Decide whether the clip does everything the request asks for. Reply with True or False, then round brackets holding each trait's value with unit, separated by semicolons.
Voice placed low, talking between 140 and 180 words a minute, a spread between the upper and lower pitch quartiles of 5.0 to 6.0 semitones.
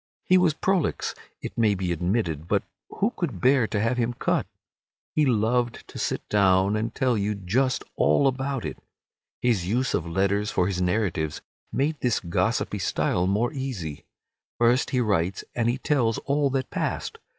True (115 Hz; 170 wpm; 5.6 semitones)